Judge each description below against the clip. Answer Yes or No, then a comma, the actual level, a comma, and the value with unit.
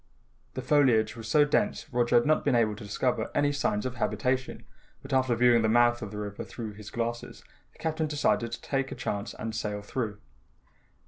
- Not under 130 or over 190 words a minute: No, average, 200 wpm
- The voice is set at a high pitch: No, low, 120 Hz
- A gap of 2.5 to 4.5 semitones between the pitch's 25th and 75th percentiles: Yes, average, 3.3 semitones